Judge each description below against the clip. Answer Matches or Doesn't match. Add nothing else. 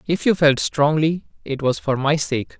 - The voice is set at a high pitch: Doesn't match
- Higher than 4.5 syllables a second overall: Doesn't match